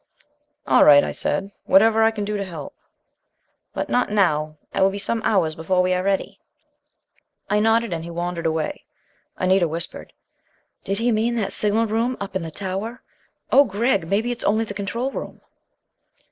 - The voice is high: Yes, high, 200 Hz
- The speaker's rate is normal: Yes, average, 175 wpm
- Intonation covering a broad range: No, average, 4.1 semitones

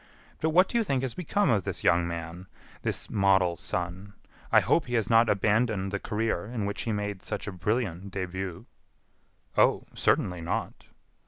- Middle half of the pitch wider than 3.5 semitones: Yes, average, 4.2 semitones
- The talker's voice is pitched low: Yes, low, 100 Hz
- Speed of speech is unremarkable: Yes, average, 175 wpm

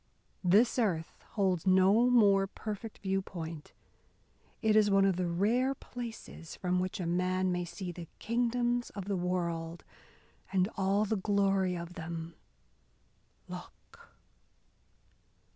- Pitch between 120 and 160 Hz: No, high, 190 Hz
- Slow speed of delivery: Yes, slow, 125 wpm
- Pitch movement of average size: Yes, average, 3.2 semitones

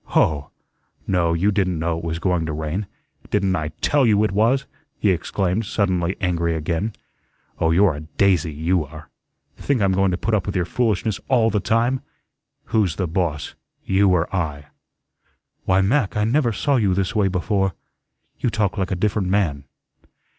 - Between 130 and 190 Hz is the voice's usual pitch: No, very low, 95 Hz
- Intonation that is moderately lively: Yes, average, 3.9 semitones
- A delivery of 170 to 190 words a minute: Yes, average, 175 wpm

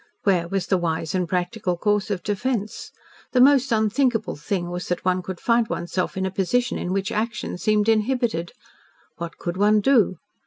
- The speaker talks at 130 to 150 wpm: No, average, 185 wpm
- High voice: Yes, high, 195 Hz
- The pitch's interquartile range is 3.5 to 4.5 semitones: Yes, average, 3.8 semitones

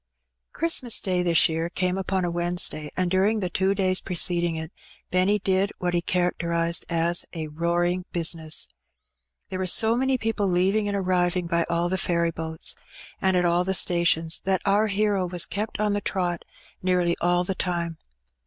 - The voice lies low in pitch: No, medium, 180 Hz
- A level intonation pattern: Yes, narrow, 2.0 semitones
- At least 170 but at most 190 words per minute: Yes, average, 180 wpm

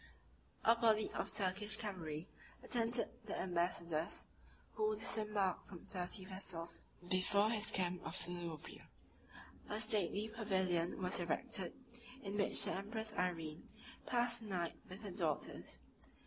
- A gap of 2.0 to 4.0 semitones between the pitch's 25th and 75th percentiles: Yes, average, 3.6 semitones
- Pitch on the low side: No, high, 190 Hz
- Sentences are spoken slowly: Yes, slow, 130 wpm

